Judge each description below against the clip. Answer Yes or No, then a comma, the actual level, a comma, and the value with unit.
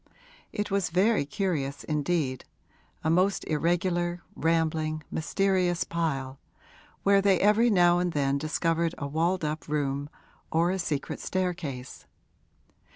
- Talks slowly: Yes, slow, 120 wpm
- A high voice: No, medium, 165 Hz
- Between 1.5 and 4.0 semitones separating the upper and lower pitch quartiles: Yes, average, 3.4 semitones